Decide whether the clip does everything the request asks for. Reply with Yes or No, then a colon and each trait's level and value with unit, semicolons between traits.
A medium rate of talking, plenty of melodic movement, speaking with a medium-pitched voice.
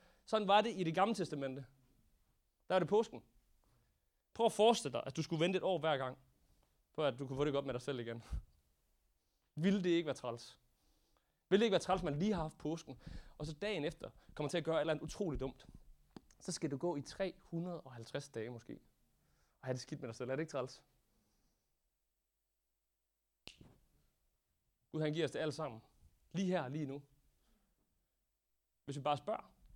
Yes: average, 200 wpm; wide, 5.8 semitones; medium, 150 Hz